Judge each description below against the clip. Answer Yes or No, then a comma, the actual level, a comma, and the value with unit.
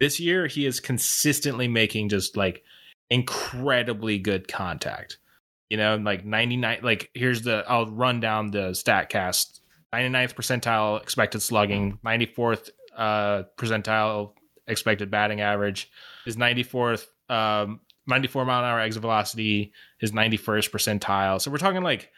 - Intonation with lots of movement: No, average, 2.9 semitones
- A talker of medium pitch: No, low, 110 Hz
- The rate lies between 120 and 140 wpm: Yes, slow, 135 wpm